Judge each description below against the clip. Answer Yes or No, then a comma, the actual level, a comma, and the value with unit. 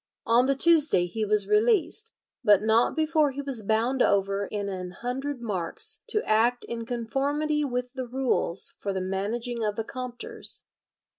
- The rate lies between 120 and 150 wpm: No, average, 160 wpm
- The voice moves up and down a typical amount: Yes, average, 5.0 semitones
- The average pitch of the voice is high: Yes, high, 240 Hz